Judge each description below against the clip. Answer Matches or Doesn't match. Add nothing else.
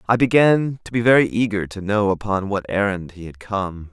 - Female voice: Doesn't match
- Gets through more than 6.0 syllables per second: Doesn't match